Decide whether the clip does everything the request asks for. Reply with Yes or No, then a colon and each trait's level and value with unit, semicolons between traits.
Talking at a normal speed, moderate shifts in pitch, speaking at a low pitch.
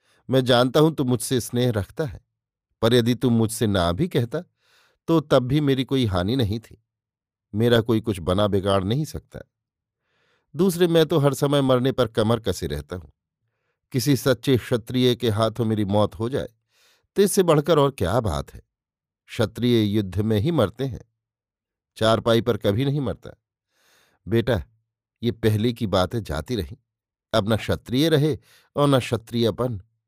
Yes: average, 165 wpm; average, 3.6 semitones; low, 115 Hz